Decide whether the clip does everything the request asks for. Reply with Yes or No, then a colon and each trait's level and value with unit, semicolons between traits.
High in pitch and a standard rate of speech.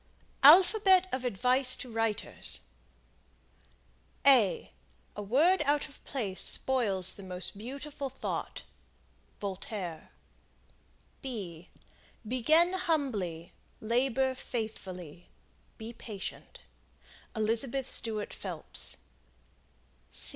No: high, 235 Hz; slow, 75 wpm